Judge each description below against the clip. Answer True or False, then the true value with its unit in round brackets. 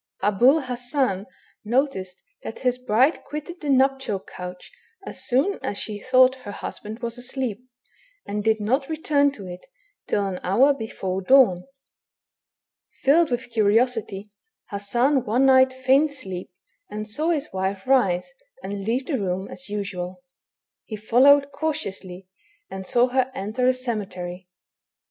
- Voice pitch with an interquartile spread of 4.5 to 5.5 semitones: True (5.1 semitones)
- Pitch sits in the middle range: False (240 Hz)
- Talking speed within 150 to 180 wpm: False (140 wpm)